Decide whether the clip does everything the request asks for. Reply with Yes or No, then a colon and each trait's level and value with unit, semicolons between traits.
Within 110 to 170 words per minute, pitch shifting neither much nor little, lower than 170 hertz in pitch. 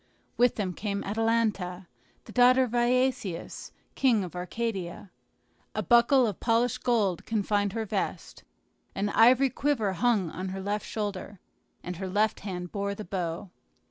No: average, 145 wpm; average, 3.8 semitones; high, 210 Hz